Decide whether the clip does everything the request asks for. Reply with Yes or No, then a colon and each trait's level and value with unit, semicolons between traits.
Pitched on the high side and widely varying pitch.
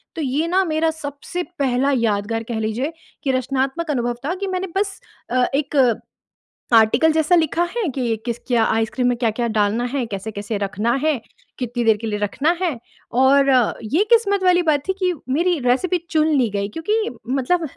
Yes: very high, 265 Hz; wide, 6.3 semitones